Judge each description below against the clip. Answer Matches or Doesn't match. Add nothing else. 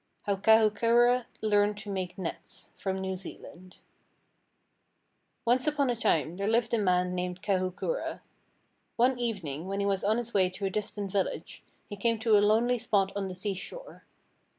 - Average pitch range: Matches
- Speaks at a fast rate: Doesn't match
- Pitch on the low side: Doesn't match